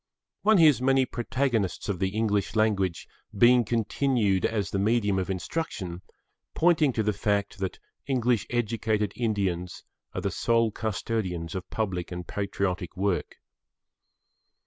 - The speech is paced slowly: Yes, slow, 130 wpm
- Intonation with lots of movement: No, average, 3.9 semitones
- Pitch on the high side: No, low, 105 Hz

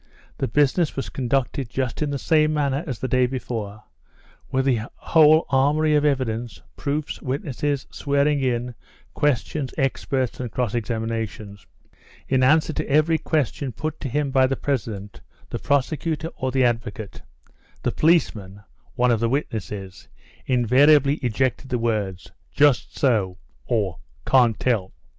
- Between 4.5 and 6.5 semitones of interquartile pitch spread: No, average, 4.0 semitones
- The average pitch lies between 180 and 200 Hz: No, low, 130 Hz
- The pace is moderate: Yes, average, 145 wpm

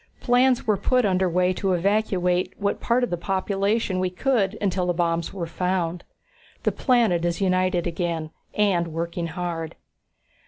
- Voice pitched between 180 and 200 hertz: Yes, medium, 185 Hz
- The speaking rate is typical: Yes, average, 155 wpm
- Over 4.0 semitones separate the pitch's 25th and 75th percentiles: No, average, 2.8 semitones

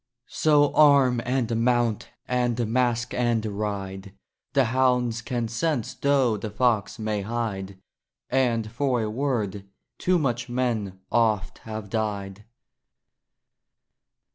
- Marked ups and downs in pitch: No, average, 3.0 semitones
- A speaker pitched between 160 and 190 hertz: No, low, 115 Hz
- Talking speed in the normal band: No, slow, 115 wpm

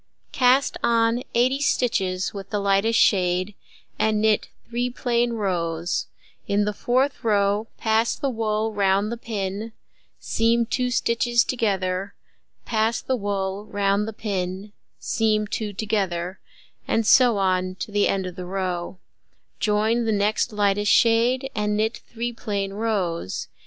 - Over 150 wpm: No, average, 140 wpm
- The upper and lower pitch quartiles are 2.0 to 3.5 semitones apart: Yes, average, 2.9 semitones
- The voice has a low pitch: No, high, 210 Hz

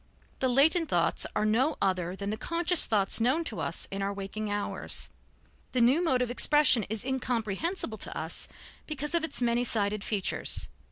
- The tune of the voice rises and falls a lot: Yes, wide, 6.2 semitones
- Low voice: No, high, 240 Hz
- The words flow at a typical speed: Yes, average, 175 wpm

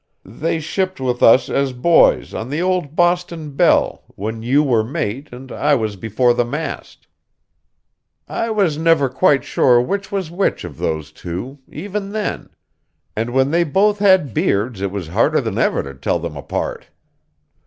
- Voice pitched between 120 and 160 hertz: Yes, medium, 140 Hz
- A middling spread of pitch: No, wide, 7.0 semitones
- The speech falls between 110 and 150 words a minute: No, average, 165 wpm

